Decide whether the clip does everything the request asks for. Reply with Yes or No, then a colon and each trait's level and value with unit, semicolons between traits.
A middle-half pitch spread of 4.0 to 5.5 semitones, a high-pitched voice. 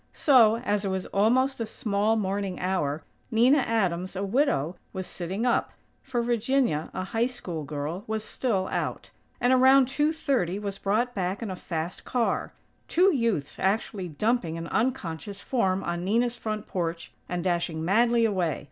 Yes: average, 4.9 semitones; high, 205 Hz